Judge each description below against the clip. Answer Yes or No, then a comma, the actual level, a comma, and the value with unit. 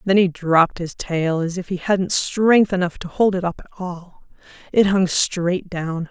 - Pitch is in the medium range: Yes, medium, 180 Hz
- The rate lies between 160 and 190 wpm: No, fast, 205 wpm